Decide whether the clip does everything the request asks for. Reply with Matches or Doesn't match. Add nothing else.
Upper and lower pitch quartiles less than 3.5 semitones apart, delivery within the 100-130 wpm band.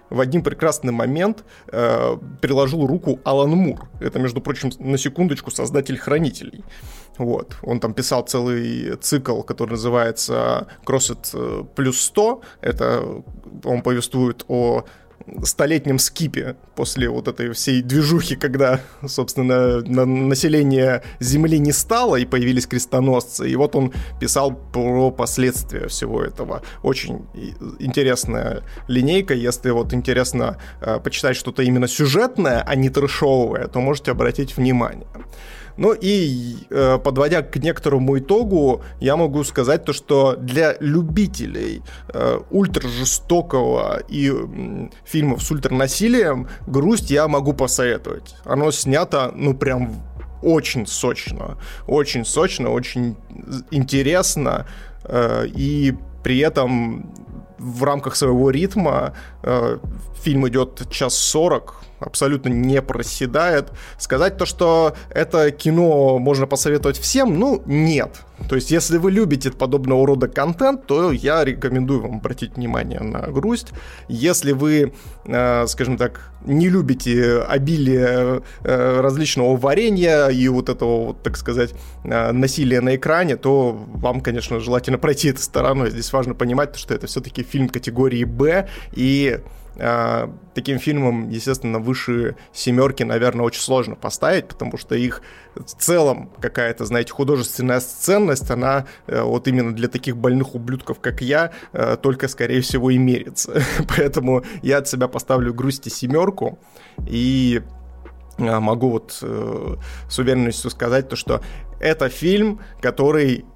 Matches